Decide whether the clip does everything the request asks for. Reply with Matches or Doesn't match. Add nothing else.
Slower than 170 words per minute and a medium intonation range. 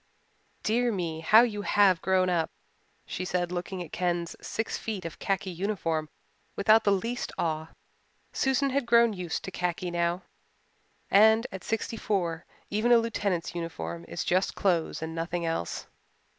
Matches